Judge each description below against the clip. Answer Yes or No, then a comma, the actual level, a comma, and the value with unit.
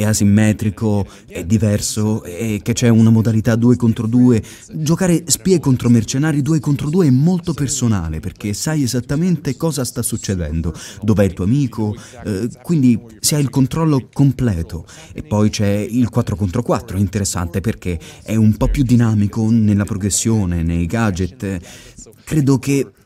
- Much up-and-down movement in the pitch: No, average, 4.2 semitones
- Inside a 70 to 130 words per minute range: No, average, 155 wpm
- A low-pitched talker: Yes, low, 115 Hz